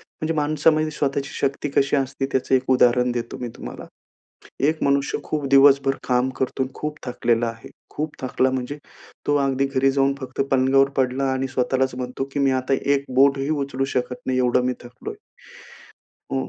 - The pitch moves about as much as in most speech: No, narrow, 1.6 semitones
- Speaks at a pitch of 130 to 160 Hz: Yes, low, 135 Hz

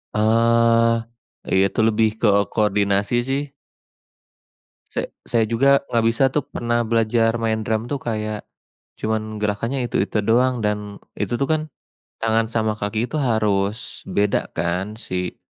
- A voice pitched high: No, low, 110 Hz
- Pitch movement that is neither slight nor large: No, narrow, 1.8 semitones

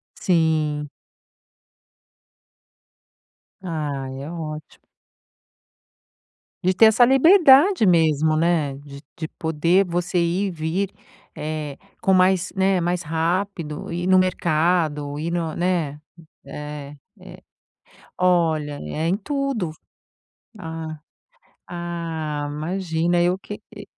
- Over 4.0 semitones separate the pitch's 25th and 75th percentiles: No, average, 3.2 semitones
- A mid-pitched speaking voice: Yes, medium, 170 Hz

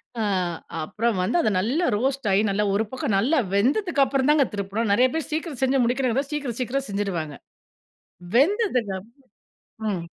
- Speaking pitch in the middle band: No, high, 245 Hz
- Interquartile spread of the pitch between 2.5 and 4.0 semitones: No, average, 5.1 semitones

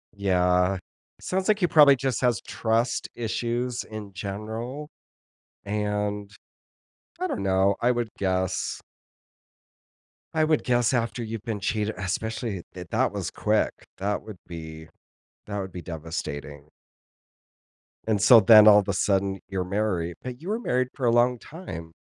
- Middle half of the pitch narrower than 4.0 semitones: No, average, 4.3 semitones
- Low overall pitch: Yes, low, 105 Hz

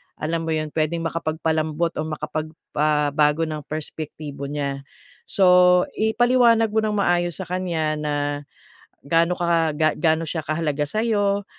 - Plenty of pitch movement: No, average, 2.9 semitones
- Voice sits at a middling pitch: Yes, medium, 160 Hz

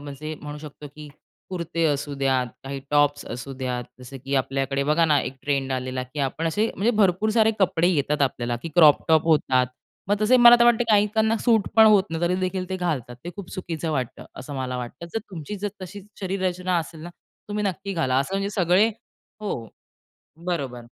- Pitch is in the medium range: Yes, medium, 165 Hz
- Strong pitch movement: Yes, wide, 5.9 semitones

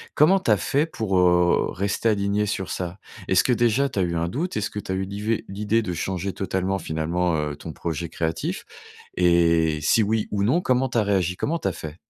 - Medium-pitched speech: No, very low, 95 Hz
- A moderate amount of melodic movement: Yes, average, 4.1 semitones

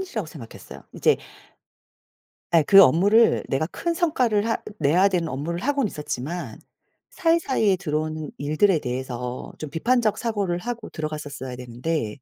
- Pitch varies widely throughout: Yes, wide, 7.2 semitones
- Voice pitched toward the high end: No, medium, 170 Hz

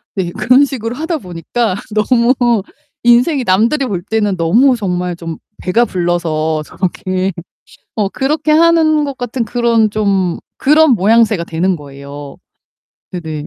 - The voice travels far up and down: Yes, wide, 6.2 semitones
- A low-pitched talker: No, high, 215 Hz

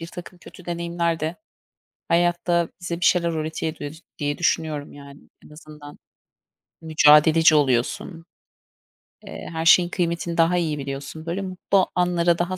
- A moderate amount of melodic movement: No, narrow, 2.2 semitones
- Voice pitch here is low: No, medium, 165 Hz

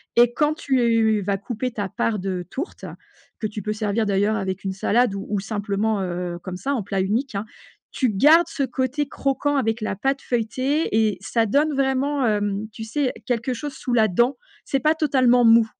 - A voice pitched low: No, high, 230 Hz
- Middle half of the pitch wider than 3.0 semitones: Yes, average, 4.7 semitones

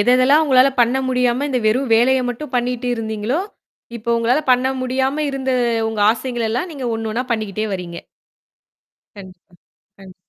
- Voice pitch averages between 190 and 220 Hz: No, high, 245 Hz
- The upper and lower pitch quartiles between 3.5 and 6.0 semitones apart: No, average, 2.9 semitones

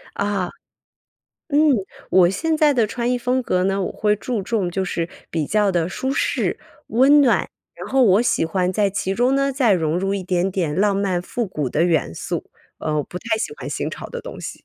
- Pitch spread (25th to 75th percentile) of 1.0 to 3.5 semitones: No, average, 5.3 semitones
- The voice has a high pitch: Yes, high, 195 Hz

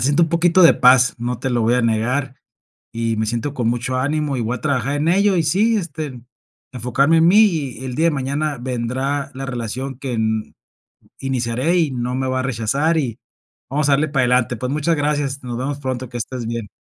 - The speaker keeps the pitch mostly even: No, average, 3.2 semitones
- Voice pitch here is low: Yes, low, 130 Hz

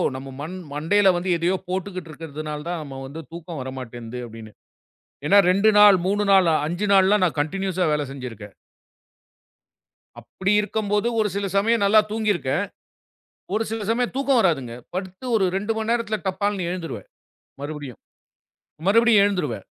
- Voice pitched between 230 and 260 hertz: No, medium, 185 Hz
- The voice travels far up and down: Yes, wide, 5.7 semitones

